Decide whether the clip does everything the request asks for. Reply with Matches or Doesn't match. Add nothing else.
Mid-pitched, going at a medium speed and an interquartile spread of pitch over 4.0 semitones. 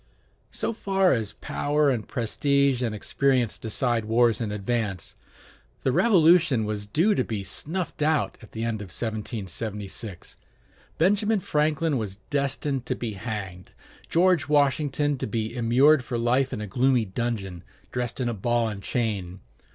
Doesn't match